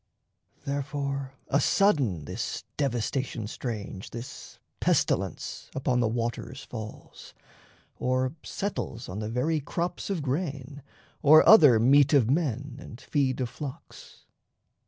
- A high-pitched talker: No, low, 135 Hz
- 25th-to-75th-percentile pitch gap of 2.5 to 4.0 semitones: Yes, average, 3.5 semitones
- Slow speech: Yes, slow, 115 wpm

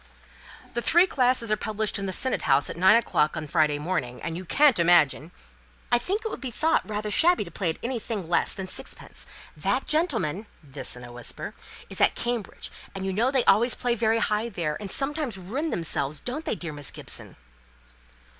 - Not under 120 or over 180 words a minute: No, fast, 205 wpm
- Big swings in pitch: Yes, wide, 6.8 semitones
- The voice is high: Yes, high, 210 Hz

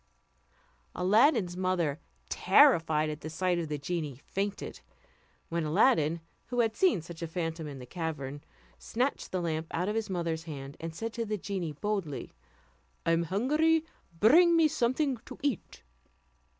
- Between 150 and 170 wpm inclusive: Yes, average, 155 wpm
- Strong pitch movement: Yes, wide, 6.0 semitones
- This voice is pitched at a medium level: Yes, medium, 175 Hz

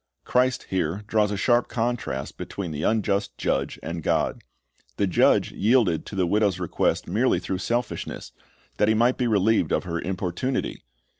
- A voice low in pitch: Yes, low, 100 Hz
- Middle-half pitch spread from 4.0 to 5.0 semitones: Yes, average, 4.3 semitones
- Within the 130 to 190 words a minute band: Yes, average, 160 wpm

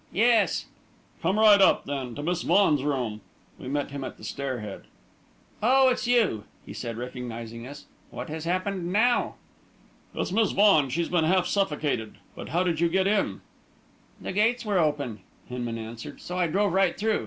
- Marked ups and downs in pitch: Yes, wide, 7.7 semitones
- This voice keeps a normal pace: Yes, average, 175 wpm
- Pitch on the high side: No, medium, 170 Hz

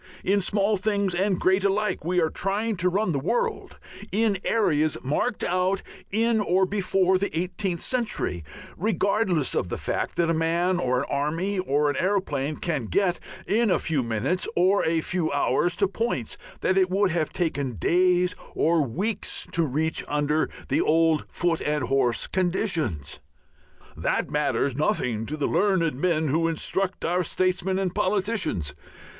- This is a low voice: No, medium, 180 Hz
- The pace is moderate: Yes, average, 160 wpm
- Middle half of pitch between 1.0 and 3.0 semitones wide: No, average, 4.3 semitones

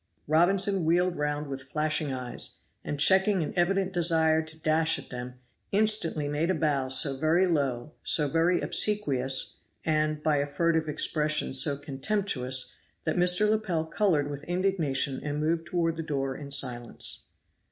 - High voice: No, medium, 155 Hz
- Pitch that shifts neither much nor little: Yes, average, 3.7 semitones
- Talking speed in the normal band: Yes, average, 150 wpm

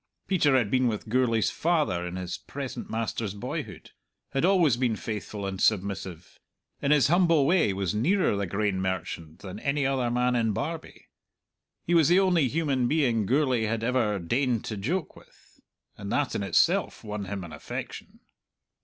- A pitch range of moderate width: No, wide, 6.2 semitones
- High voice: No, low, 115 Hz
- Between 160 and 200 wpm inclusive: Yes, average, 170 wpm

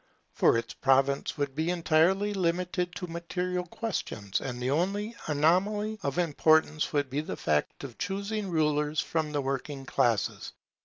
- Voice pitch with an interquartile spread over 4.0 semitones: Yes, average, 4.5 semitones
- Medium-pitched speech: Yes, medium, 160 Hz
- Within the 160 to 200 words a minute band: No, average, 150 wpm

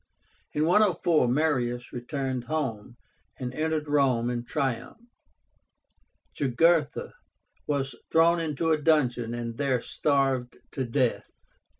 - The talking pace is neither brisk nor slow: No, slow, 105 wpm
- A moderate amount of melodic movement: Yes, average, 4.2 semitones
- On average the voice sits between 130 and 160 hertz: Yes, medium, 140 Hz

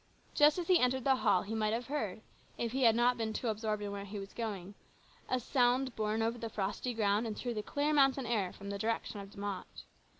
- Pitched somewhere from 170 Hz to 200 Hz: No, high, 225 Hz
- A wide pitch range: No, average, 3.4 semitones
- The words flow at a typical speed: No, fast, 240 wpm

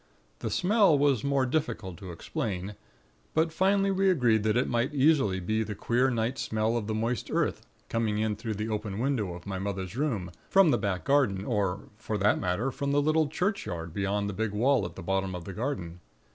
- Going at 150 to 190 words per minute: No, fast, 205 wpm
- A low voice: Yes, low, 110 Hz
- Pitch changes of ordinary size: No, wide, 6.2 semitones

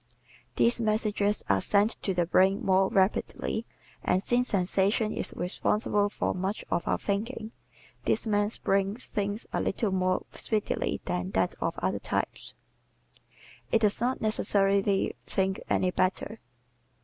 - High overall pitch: Yes, high, 200 Hz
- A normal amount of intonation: No, narrow, 2.1 semitones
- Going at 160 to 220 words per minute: No, slow, 135 wpm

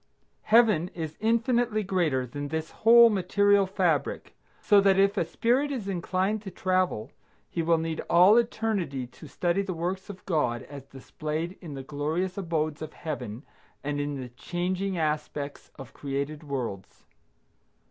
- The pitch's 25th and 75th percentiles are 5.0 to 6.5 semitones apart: Yes, average, 5.3 semitones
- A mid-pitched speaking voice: Yes, medium, 170 Hz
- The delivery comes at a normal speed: Yes, average, 150 wpm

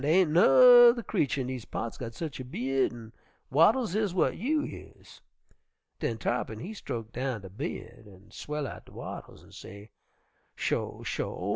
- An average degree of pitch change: No, wide, 8.1 semitones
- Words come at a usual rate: Yes, average, 170 wpm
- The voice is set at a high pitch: No, low, 135 Hz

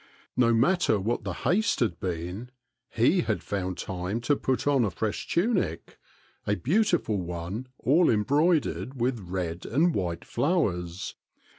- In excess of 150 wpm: No, average, 145 wpm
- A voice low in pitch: Yes, low, 115 Hz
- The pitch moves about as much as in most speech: No, wide, 7.9 semitones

